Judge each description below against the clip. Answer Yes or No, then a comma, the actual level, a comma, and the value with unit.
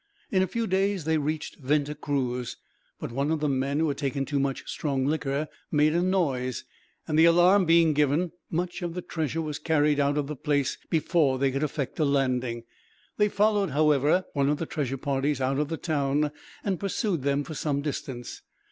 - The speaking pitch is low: No, medium, 150 Hz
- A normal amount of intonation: Yes, average, 3.0 semitones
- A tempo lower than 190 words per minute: No, average, 200 wpm